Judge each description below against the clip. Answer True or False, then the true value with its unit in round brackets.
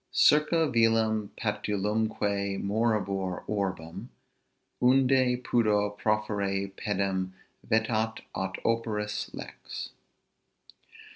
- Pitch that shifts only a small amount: True (2.3 semitones)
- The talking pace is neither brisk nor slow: False (70 wpm)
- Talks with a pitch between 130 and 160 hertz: False (105 Hz)